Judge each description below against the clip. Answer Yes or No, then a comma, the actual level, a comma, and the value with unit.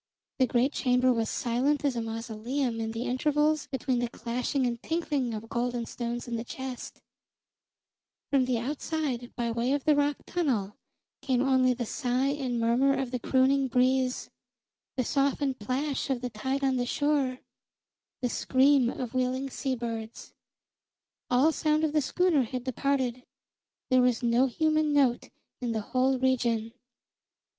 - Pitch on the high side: Yes, very high, 255 Hz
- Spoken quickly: No, average, 155 wpm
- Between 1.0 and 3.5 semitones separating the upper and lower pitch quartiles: Yes, narrow, 2.5 semitones